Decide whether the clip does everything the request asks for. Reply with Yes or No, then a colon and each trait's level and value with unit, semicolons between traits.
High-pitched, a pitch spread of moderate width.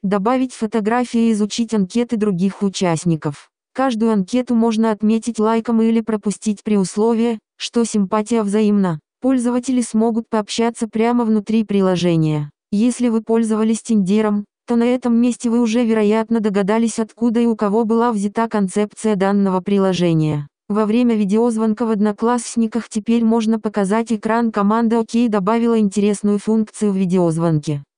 No: high, 220 Hz; narrow, 2.1 semitones